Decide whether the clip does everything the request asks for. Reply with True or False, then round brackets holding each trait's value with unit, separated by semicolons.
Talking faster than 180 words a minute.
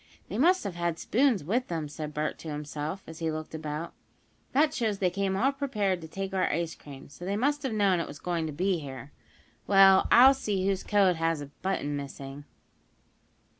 True (205 wpm)